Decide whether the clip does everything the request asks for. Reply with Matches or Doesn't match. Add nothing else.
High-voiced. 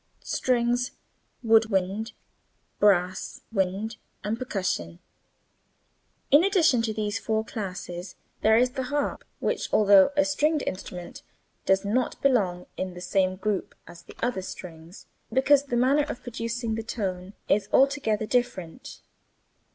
Matches